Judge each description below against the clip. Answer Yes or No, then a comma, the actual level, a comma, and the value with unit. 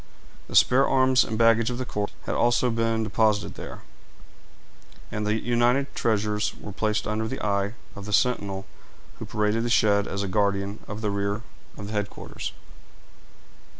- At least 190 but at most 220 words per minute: No, average, 165 wpm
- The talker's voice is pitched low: Yes, low, 110 Hz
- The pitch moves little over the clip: Yes, narrow, 2.3 semitones